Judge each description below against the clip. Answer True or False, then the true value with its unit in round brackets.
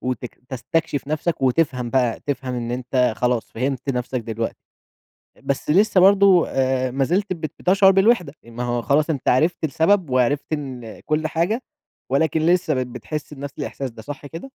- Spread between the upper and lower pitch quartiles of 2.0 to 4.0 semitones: False (4.4 semitones)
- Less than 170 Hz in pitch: True (140 Hz)